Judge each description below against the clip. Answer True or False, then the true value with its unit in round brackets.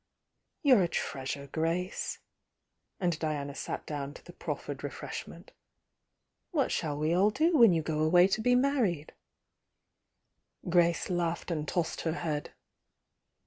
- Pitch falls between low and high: True (170 Hz)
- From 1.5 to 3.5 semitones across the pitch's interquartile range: False (4.1 semitones)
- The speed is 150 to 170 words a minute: False (140 wpm)